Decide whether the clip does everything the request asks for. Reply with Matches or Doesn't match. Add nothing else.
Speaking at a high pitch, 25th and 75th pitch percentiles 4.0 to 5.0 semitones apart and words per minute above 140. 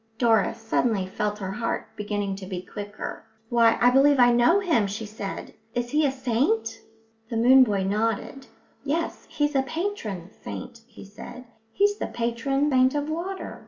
Matches